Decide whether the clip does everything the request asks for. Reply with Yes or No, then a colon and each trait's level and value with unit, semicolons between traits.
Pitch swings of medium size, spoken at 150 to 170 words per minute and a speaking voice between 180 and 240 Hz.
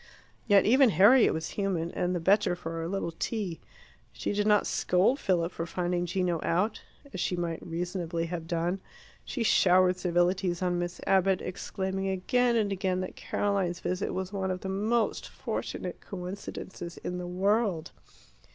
No: narrow, 2.2 semitones; average, 160 wpm; medium, 185 Hz